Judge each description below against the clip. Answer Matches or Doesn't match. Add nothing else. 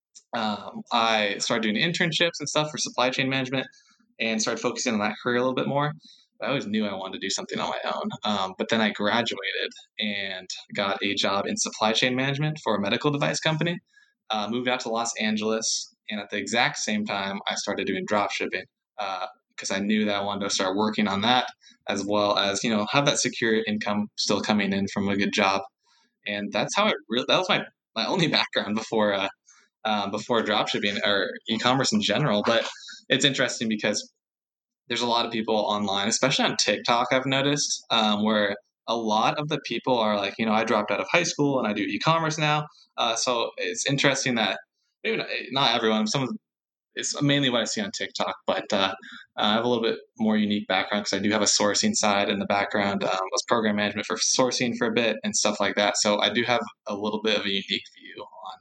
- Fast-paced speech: Matches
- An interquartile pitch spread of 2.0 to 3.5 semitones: Doesn't match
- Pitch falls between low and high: Doesn't match